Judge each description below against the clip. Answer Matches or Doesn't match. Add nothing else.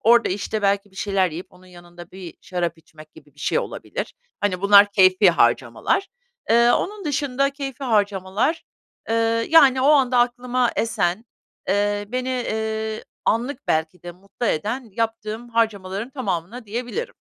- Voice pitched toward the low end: Doesn't match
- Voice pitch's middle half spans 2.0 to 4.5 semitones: Doesn't match